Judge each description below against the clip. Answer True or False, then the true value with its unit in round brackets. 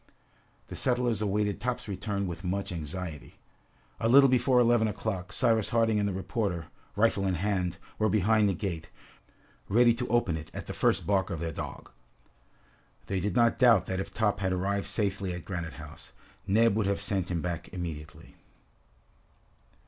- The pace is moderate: True (170 wpm)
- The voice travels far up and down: False (3.7 semitones)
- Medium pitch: False (100 Hz)